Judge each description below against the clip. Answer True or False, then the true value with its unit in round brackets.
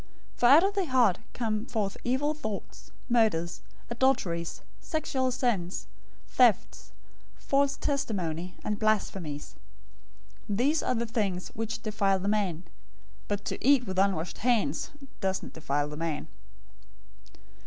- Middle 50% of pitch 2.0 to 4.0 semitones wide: False (5.6 semitones)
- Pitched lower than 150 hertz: False (215 Hz)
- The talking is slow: True (130 wpm)